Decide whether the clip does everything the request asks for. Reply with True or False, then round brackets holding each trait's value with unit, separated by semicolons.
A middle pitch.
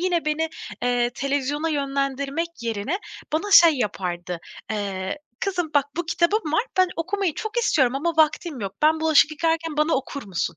False (300 Hz)